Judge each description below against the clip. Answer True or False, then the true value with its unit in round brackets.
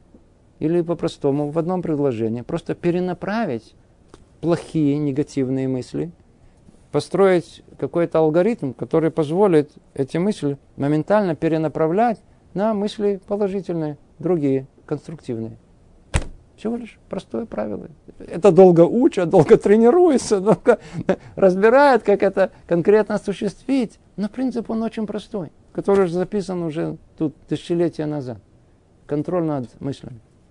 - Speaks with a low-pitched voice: False (170 Hz)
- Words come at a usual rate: False (105 wpm)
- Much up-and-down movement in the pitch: True (5.8 semitones)